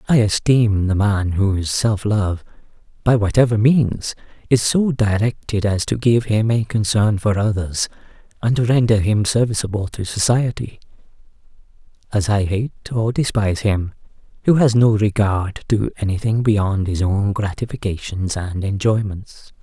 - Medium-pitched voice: No, low, 105 Hz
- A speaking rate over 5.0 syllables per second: No, 4.4 syllables/s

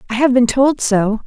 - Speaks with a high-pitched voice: Yes, high, 245 Hz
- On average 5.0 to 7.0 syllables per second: No, 4.7 syllables/s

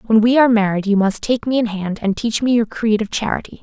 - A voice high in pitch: Yes, high, 220 Hz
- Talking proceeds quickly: Yes, fast, 280 wpm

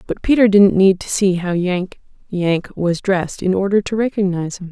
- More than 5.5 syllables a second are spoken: No, 5.1 syllables/s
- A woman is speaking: Yes, female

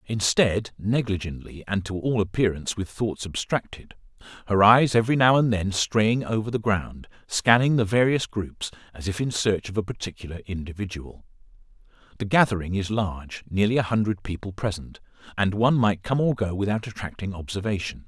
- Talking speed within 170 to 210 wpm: No, average, 155 wpm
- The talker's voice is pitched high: No, low, 105 Hz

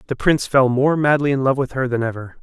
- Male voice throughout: Yes, male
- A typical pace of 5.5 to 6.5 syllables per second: Yes, 6.3 syllables/s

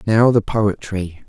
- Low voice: Yes, low, 105 Hz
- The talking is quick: No, average, 140 wpm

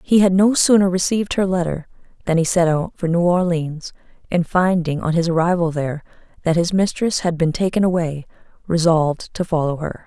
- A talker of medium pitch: Yes, medium, 170 Hz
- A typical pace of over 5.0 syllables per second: Yes, 5.5 syllables/s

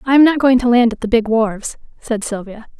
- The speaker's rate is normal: No, fast, 255 wpm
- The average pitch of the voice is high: Yes, high, 235 Hz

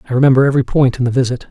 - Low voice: Yes, low, 130 Hz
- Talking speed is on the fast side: Yes, fast, 280 wpm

